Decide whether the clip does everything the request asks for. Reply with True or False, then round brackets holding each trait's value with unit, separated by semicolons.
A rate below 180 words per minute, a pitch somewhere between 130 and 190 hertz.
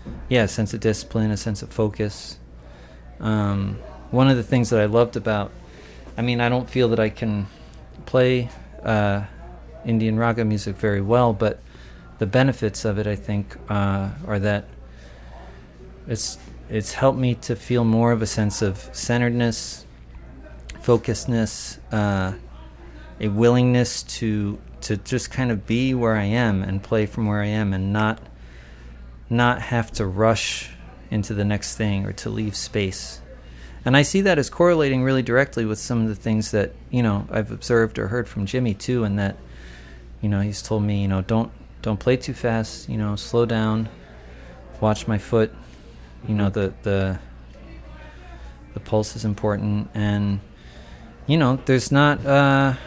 False (165 wpm; 105 Hz)